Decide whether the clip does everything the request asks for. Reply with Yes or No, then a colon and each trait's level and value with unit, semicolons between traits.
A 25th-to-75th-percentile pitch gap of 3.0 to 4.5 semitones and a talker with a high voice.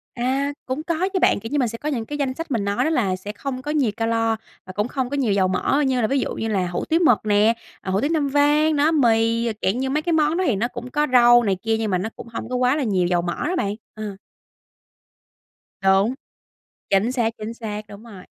No: average, 5.2 semitones; high, 235 Hz